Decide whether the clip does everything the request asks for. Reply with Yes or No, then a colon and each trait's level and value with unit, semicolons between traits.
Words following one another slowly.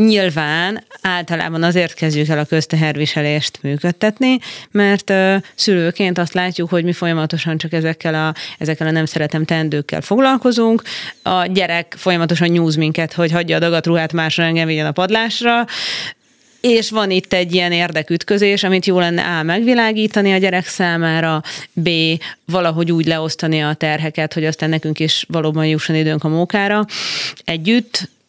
No: average, 145 wpm